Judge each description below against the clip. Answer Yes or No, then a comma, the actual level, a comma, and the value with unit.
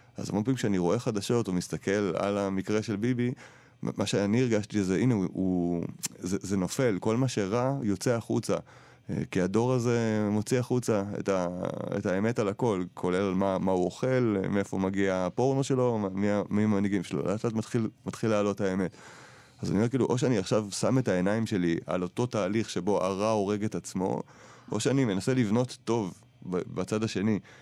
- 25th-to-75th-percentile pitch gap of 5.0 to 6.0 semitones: No, average, 3.8 semitones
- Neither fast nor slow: No, fast, 175 wpm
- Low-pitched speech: Yes, low, 105 Hz